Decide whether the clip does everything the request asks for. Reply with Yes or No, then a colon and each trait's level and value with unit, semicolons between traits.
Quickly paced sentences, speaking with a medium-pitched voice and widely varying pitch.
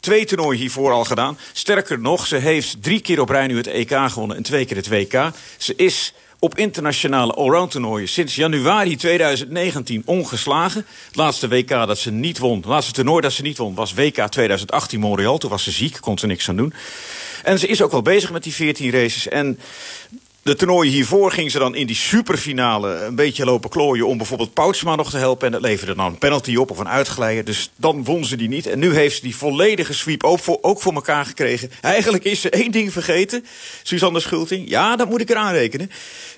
Yes: fast, 215 wpm; medium, 145 Hz; wide, 6.0 semitones